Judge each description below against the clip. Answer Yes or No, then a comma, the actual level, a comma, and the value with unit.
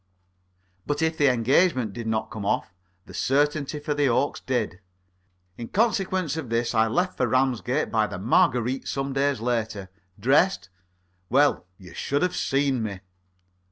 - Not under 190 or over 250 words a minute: No, average, 155 wpm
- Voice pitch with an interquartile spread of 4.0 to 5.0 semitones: Yes, average, 4.6 semitones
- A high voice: No, low, 130 Hz